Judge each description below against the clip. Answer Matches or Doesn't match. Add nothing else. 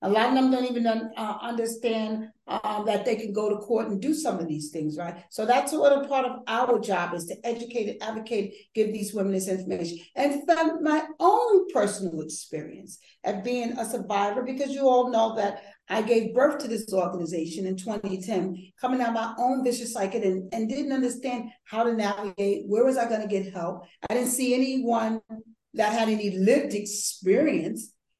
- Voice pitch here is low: Doesn't match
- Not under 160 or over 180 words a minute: Doesn't match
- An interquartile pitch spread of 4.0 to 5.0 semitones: Doesn't match